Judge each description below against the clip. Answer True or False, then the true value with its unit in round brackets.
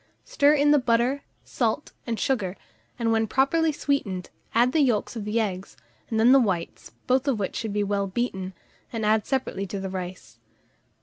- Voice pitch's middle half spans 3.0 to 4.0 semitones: False (5.0 semitones)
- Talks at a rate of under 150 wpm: False (185 wpm)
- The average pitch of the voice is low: False (225 Hz)